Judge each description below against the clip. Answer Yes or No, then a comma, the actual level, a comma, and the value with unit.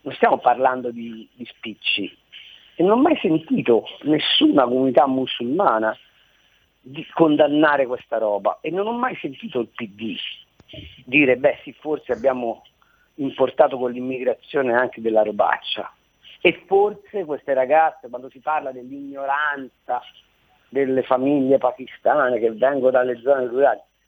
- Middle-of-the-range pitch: No, low, 130 Hz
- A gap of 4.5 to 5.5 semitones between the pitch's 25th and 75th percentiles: No, average, 3.3 semitones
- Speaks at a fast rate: No, average, 130 wpm